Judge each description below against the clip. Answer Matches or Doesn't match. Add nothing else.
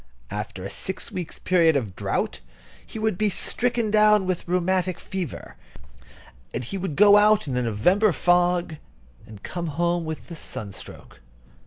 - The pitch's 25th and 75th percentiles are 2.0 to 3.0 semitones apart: Doesn't match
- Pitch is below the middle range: Doesn't match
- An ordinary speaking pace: Matches